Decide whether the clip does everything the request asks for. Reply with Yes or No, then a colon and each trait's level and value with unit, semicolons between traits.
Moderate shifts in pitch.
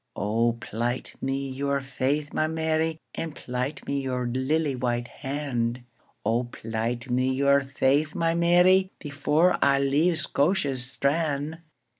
Yes: average, 3.8 semitones